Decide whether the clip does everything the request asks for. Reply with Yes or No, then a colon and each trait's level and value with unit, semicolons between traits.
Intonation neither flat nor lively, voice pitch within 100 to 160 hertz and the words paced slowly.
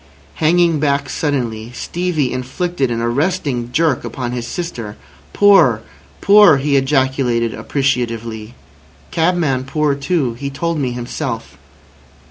Yes: average, 4.9 semitones; low, 135 Hz; slow, 110 wpm